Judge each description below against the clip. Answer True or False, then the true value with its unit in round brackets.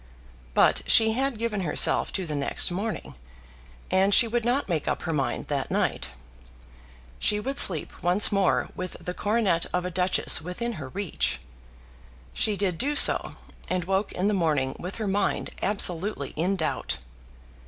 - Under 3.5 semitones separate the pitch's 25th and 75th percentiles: False (3.9 semitones)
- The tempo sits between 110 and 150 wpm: False (165 wpm)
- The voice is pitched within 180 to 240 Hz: True (190 Hz)